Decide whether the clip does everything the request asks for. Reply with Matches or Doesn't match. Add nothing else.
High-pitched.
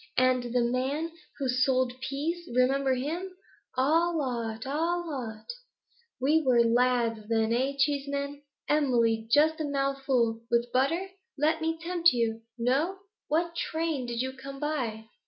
Matches